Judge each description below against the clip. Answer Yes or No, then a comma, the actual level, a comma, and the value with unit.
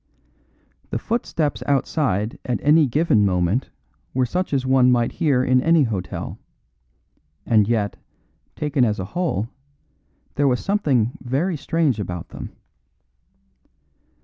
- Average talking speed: No, slow, 120 wpm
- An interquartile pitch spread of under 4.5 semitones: No, wide, 5.5 semitones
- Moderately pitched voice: No, low, 130 Hz